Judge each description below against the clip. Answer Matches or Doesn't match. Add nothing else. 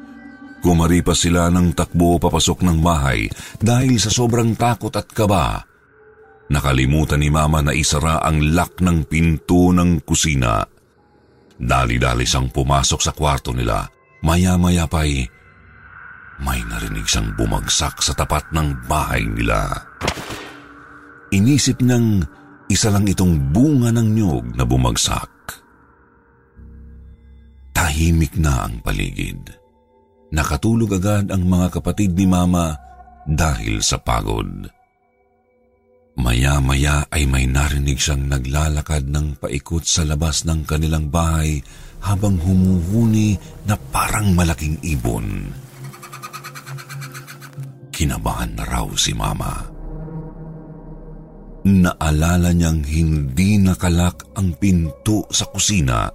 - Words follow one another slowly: Matches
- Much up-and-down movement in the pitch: Matches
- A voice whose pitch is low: Matches